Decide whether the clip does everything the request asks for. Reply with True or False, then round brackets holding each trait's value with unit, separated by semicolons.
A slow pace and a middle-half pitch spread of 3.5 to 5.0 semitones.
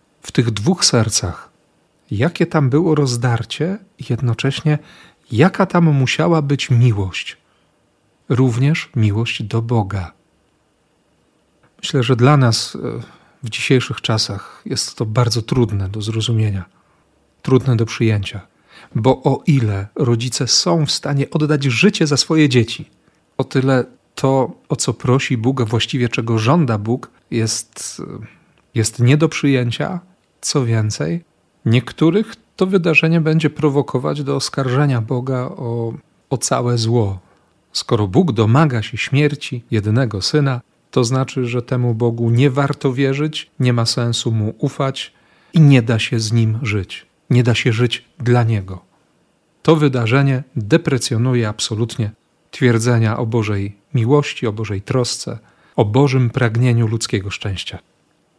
False (130 wpm; 4.2 semitones)